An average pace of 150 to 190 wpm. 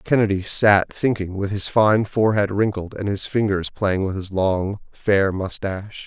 Yes: average, 170 wpm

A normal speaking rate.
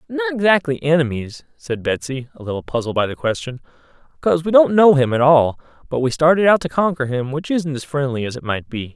No: fast, 220 wpm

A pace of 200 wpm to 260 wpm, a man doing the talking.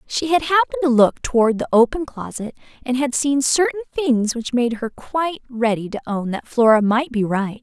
No: fast, 205 wpm; female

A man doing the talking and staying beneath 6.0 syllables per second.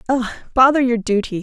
No: female; 5.7 syllables/s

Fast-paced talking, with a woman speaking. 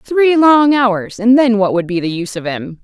Yes: fast, 255 wpm; female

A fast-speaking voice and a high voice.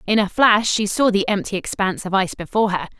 Yes: fast, 240 wpm; high, 200 Hz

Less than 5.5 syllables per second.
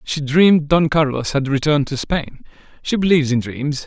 Yes: 5.3 syllables/s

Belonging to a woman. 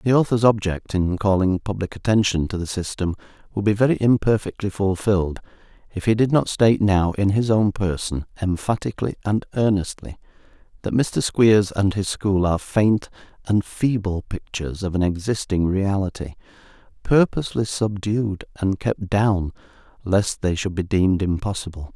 No: male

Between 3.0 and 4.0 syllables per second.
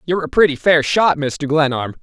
No: 5.5 syllables/s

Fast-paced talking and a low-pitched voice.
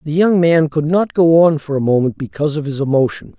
No: fast, 250 wpm; medium, 155 Hz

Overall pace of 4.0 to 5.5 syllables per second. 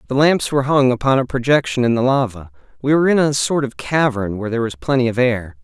No: 6.5 syllables/s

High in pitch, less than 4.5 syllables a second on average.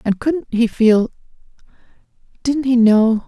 Yes: high, 240 Hz; 3.8 syllables/s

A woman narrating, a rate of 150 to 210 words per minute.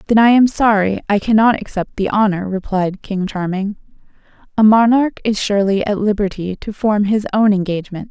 Yes: female; average, 170 wpm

